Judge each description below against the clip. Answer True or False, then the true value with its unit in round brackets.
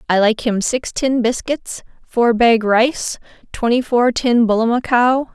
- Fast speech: False (145 wpm)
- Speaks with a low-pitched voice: False (235 Hz)